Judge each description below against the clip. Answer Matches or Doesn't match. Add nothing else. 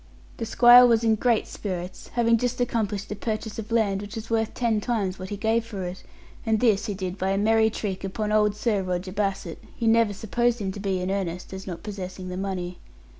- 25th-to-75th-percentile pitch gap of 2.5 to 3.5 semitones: Matches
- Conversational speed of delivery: Doesn't match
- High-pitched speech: Matches